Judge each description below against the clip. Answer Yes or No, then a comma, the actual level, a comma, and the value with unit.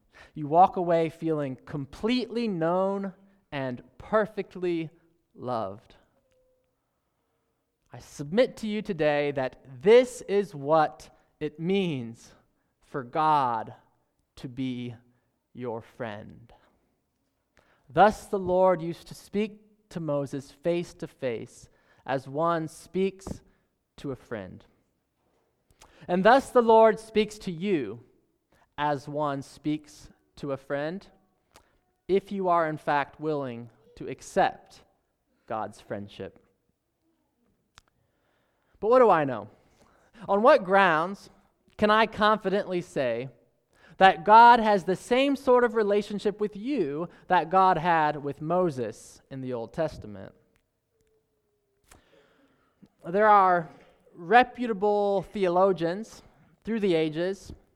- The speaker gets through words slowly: Yes, slow, 110 wpm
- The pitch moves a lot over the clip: Yes, wide, 6.2 semitones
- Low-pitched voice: No, medium, 170 Hz